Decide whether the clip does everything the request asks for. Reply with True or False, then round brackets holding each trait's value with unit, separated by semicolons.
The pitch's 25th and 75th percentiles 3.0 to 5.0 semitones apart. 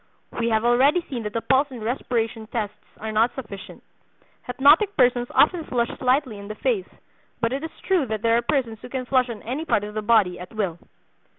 True (3.5 semitones)